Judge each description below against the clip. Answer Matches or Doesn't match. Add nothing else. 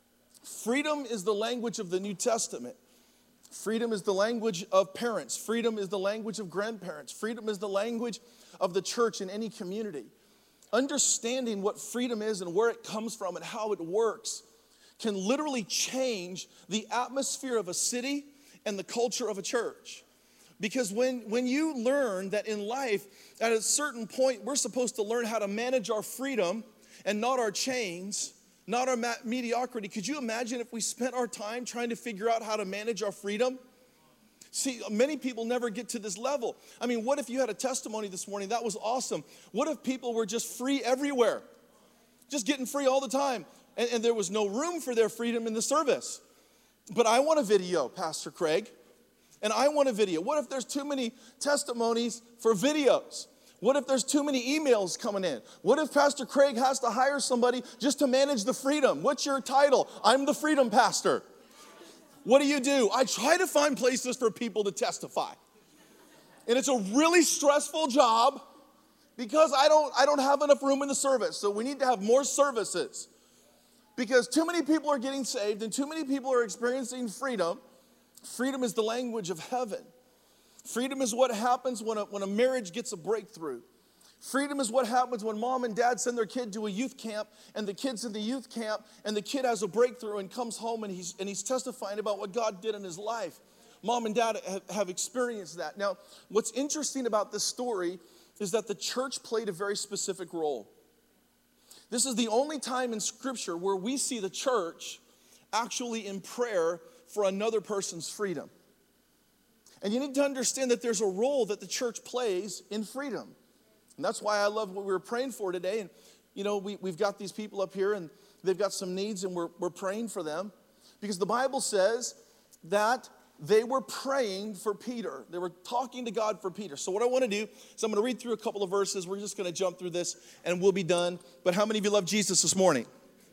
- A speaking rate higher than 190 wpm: Matches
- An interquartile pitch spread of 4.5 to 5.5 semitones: Doesn't match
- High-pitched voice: Matches